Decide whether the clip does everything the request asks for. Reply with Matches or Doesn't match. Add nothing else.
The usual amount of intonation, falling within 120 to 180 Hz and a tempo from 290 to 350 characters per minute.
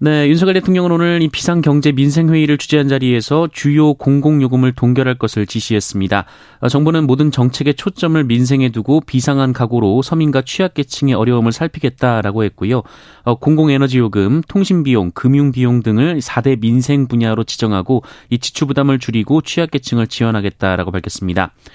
Doesn't match